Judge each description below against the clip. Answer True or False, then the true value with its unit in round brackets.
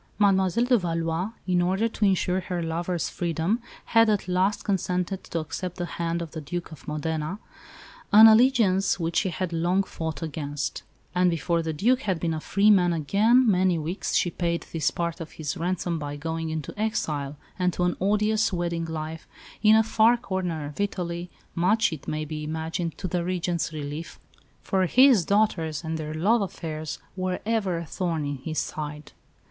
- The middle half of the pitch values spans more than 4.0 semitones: False (3.2 semitones)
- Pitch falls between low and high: True (175 Hz)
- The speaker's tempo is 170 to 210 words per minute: True (180 wpm)